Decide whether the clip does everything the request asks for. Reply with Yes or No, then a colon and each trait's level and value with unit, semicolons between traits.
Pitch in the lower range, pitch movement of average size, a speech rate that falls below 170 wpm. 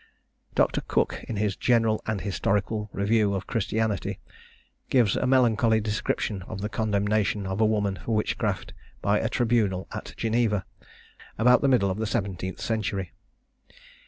No: low, 105 Hz; narrow, 2.1 semitones; average, 145 wpm